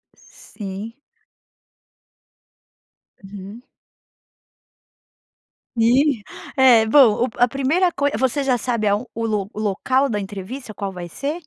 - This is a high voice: Yes, high, 230 Hz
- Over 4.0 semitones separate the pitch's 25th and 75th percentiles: Yes, average, 4.6 semitones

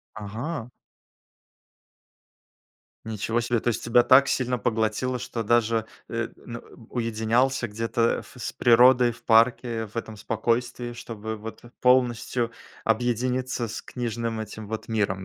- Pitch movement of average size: No, narrow, 1.7 semitones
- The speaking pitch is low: Yes, low, 115 Hz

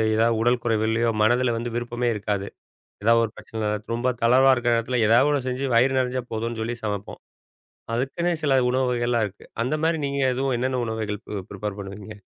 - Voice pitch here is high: No, low, 120 Hz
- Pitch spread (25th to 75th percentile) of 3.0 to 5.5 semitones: No, narrow, 2.6 semitones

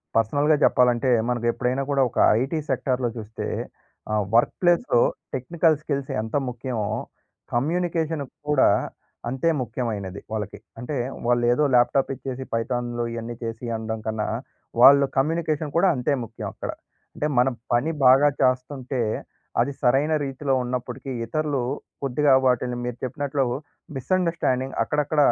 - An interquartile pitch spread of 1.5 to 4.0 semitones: Yes, average, 3.5 semitones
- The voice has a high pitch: No, low, 130 Hz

